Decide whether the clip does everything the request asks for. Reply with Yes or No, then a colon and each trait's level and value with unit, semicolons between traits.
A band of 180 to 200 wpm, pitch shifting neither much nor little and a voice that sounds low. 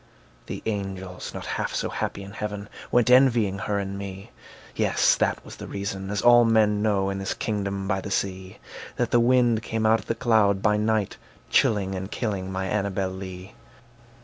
No: average, 185 wpm; narrow, 2.3 semitones; low, 100 Hz